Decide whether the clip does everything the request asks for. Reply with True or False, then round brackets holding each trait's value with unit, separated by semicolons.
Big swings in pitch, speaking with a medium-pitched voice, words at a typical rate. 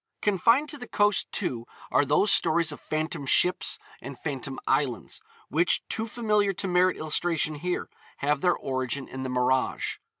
True (6.2 semitones; 155 Hz; 160 wpm)